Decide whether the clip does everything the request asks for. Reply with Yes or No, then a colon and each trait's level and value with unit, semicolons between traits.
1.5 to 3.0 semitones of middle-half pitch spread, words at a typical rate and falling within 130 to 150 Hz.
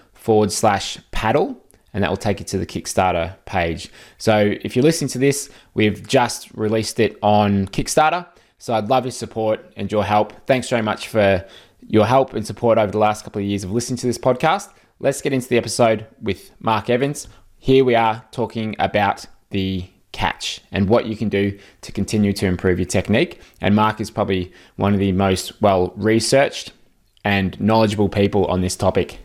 No: average, 2.7 semitones; average, 190 wpm; low, 105 Hz